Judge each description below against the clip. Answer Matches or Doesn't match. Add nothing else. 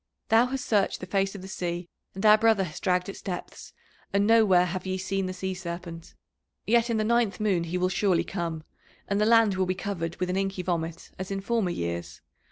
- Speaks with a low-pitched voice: Doesn't match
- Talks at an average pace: Doesn't match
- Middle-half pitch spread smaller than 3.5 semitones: Matches